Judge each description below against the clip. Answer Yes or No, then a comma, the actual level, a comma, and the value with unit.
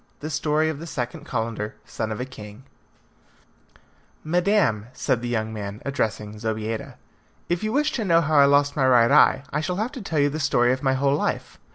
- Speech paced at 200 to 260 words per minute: Yes, fast, 205 wpm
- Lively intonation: Yes, wide, 5.8 semitones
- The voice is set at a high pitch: No, low, 135 Hz